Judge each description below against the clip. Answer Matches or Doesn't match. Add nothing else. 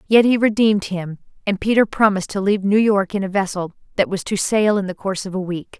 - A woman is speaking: Matches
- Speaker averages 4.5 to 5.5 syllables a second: Doesn't match